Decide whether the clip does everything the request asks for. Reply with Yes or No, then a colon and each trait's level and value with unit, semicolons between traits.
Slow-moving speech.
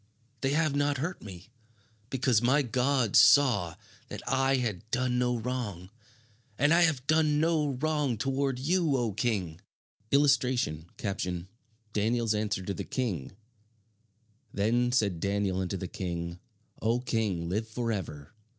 Yes: slow, 130 wpm